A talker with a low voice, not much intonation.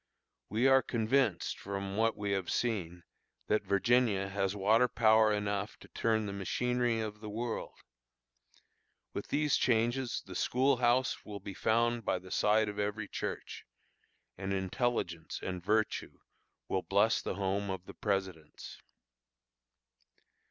No: low, 105 Hz; average, 3.3 semitones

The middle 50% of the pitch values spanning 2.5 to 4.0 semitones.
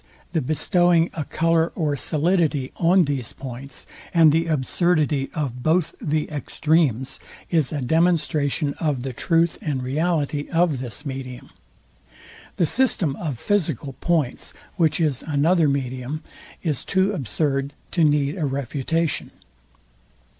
Yes: average, 3.3 semitones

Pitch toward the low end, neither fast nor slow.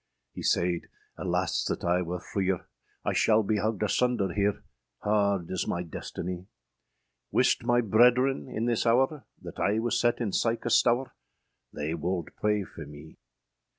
Yes: low, 105 Hz; average, 155 wpm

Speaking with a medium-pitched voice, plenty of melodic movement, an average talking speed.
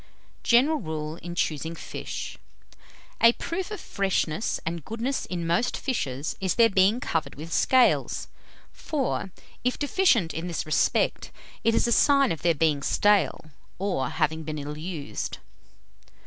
Yes: medium, 175 Hz; wide, 7.0 semitones; average, 150 wpm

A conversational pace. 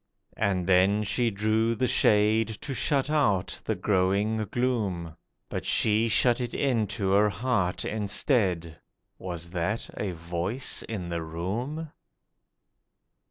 No: slow, 120 wpm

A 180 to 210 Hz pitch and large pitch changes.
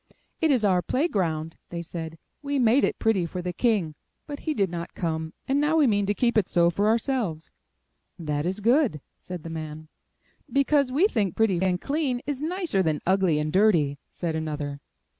Yes: high, 190 Hz; wide, 7.7 semitones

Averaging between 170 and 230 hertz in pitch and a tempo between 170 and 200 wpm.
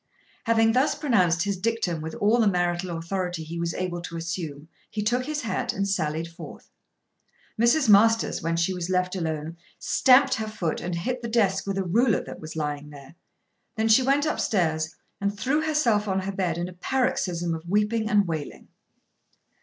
Yes: high, 190 Hz; average, 185 wpm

